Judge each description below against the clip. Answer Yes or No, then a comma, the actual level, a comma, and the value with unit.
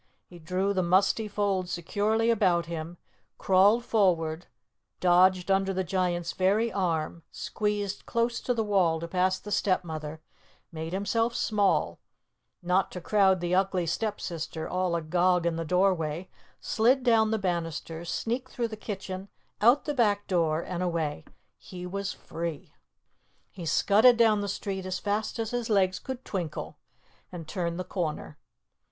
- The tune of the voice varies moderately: Yes, average, 3.3 semitones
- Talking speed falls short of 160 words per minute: Yes, average, 150 wpm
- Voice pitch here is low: No, medium, 185 Hz